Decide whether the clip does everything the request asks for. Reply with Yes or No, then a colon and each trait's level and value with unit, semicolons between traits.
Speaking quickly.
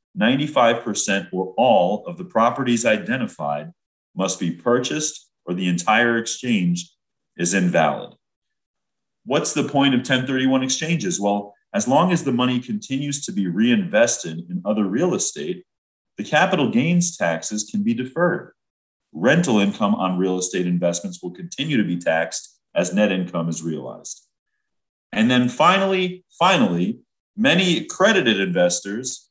No: slow, 135 wpm